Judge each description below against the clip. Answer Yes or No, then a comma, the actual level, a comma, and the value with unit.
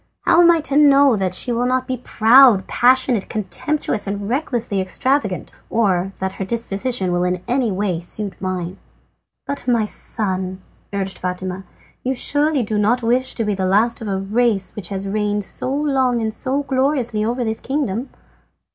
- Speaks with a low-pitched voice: No, high, 220 Hz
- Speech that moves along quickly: No, average, 175 wpm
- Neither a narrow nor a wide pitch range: Yes, average, 5.0 semitones